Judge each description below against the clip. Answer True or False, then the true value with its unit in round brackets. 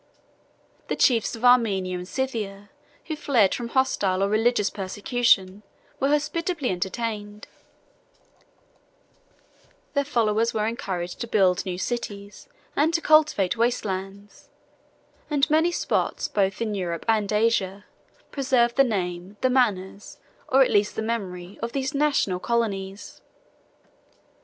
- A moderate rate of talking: False (125 wpm)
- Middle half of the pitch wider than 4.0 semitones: True (4.5 semitones)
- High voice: True (215 Hz)